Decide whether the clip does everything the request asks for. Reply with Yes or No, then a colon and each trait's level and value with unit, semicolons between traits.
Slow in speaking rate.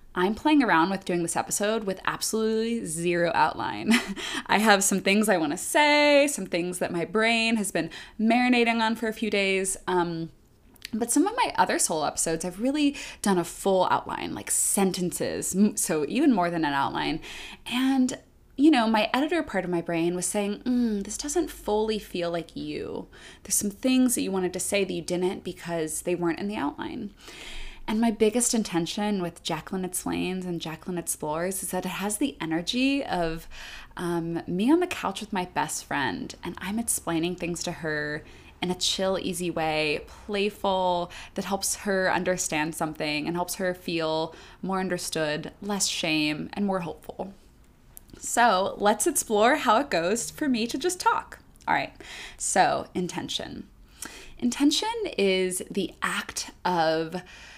No: average, 170 wpm